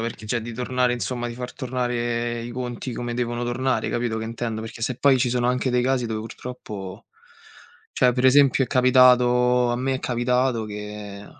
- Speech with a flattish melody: Yes, narrow, 1.4 semitones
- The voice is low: Yes, low, 120 Hz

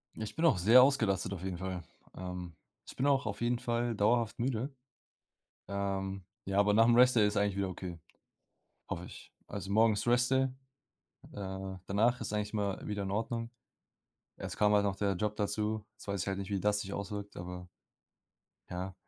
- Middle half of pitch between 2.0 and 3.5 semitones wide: Yes, average, 2.9 semitones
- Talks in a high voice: No, low, 105 Hz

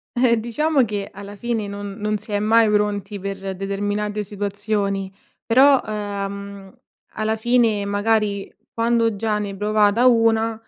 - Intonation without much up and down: Yes, narrow, 2.0 semitones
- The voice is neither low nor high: No, high, 210 Hz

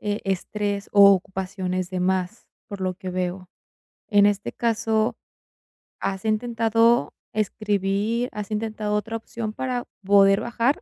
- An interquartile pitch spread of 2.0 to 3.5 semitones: Yes, average, 2.7 semitones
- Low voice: No, high, 205 Hz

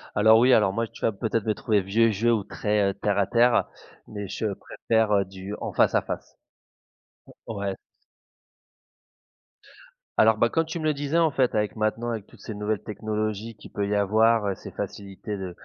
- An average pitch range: No, narrow, 2.1 semitones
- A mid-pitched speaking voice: No, low, 110 Hz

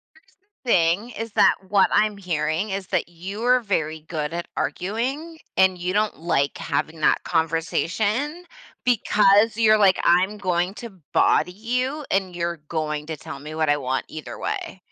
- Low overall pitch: No, high, 190 Hz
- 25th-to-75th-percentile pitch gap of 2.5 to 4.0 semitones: No, average, 4.9 semitones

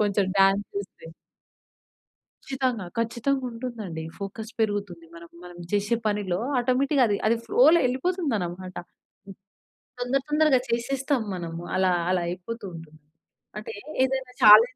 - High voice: Yes, high, 215 Hz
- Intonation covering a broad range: Yes, wide, 5.7 semitones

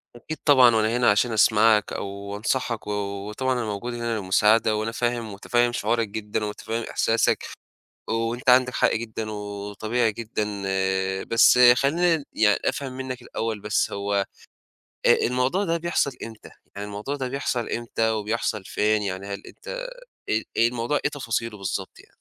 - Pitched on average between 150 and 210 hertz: No, low, 115 Hz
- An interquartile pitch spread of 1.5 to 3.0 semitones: Yes, average, 2.7 semitones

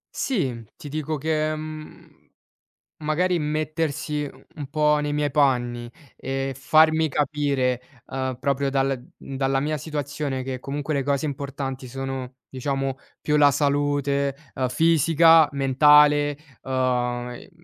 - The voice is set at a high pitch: No, medium, 140 Hz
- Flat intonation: Yes, narrow, 2.2 semitones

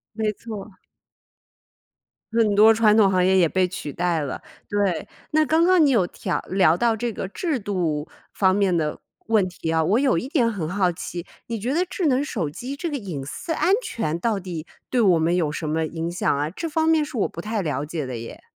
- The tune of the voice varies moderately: No, wide, 5.8 semitones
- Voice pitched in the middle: No, high, 195 Hz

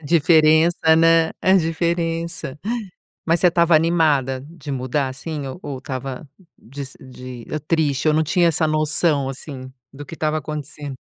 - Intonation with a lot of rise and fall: No, average, 3.3 semitones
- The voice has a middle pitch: Yes, medium, 155 Hz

